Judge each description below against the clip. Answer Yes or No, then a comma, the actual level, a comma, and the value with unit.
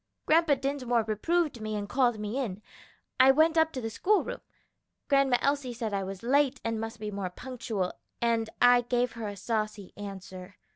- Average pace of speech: Yes, average, 185 wpm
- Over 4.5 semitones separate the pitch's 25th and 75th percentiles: No, average, 4.2 semitones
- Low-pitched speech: No, high, 235 Hz